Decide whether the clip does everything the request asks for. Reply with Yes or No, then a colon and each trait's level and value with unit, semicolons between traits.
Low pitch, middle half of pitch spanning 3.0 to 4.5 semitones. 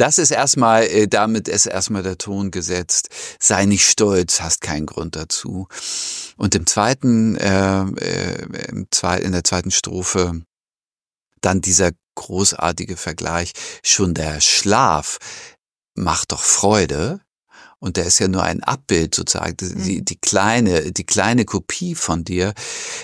No: very low, 95 Hz; narrow, 2.4 semitones